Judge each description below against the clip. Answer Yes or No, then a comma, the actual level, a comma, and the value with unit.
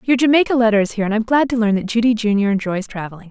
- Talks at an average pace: No, fast, 270 wpm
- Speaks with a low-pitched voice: No, high, 220 Hz